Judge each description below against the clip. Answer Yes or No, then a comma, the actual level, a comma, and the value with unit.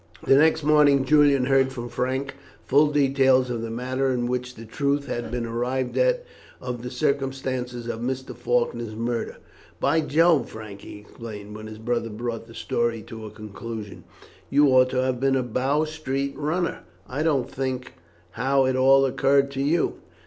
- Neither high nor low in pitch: No, low, 130 Hz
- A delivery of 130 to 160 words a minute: No, average, 175 wpm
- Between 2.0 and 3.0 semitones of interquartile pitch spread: Yes, average, 2.7 semitones